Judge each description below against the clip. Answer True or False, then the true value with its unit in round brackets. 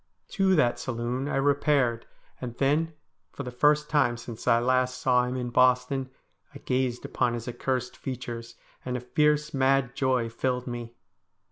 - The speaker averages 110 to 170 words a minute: True (165 wpm)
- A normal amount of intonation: False (2.1 semitones)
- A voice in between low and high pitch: False (125 Hz)